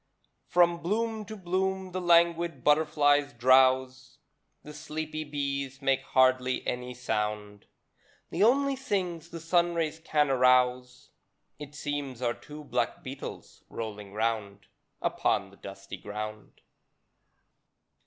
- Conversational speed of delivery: No, slow, 115 wpm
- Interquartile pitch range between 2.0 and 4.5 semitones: No, average, 5.2 semitones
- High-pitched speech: No, medium, 145 Hz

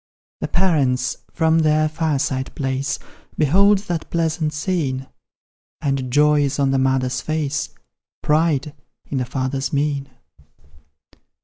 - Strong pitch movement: No, average, 2.9 semitones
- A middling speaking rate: No, slow, 115 wpm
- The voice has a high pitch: No, medium, 145 Hz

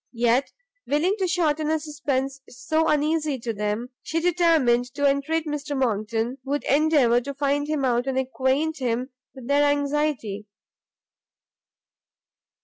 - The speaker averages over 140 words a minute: No, slow, 135 wpm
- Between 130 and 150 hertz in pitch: No, very high, 280 Hz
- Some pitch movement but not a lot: Yes, average, 3.5 semitones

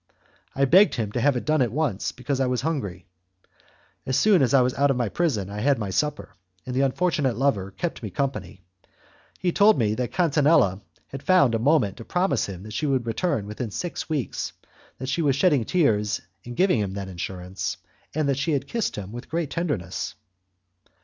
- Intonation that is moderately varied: No, wide, 6.3 semitones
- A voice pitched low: Yes, low, 130 Hz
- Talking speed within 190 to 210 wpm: Yes, fast, 205 wpm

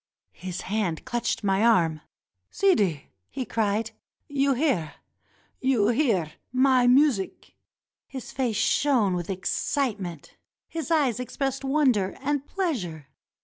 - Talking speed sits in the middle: No, slow, 115 wpm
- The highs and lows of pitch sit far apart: Yes, wide, 6.1 semitones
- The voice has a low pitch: No, high, 235 Hz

